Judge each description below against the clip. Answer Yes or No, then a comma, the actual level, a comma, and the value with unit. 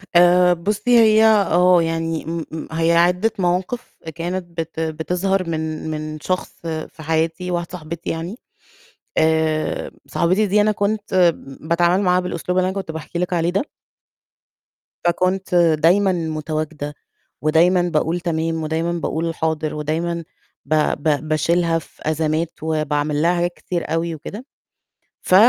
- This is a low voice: No, medium, 170 Hz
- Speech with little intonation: Yes, narrow, 2.3 semitones